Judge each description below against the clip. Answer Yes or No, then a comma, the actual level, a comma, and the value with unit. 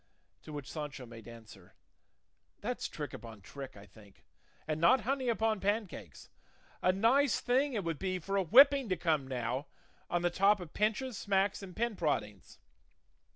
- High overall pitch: No, medium, 180 Hz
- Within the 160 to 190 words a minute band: Yes, average, 165 wpm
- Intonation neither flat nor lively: No, wide, 8.7 semitones